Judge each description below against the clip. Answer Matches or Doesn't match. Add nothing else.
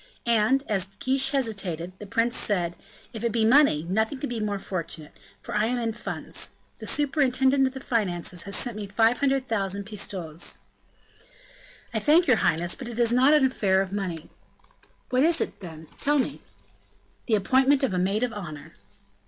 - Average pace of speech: Matches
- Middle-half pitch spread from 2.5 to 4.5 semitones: Doesn't match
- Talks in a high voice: Matches